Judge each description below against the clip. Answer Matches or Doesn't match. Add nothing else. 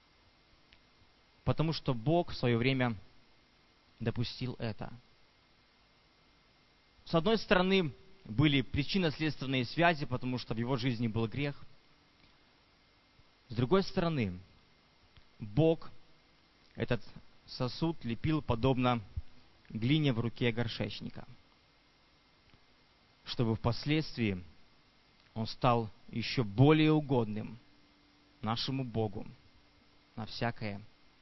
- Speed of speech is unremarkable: Doesn't match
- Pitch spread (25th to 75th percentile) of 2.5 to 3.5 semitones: Doesn't match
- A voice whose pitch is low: Matches